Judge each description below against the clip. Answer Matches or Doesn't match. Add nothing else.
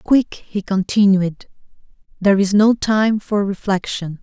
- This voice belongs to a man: Doesn't match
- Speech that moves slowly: Matches